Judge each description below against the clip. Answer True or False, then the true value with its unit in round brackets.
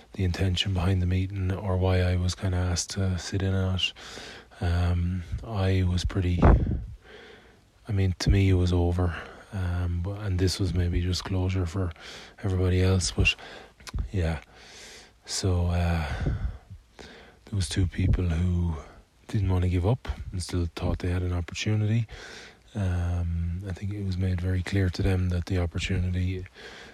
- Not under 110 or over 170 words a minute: True (165 wpm)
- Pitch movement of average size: False (1.5 semitones)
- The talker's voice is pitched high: False (90 Hz)